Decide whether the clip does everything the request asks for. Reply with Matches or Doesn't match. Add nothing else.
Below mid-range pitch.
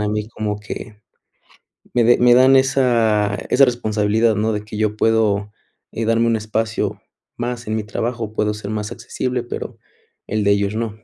Matches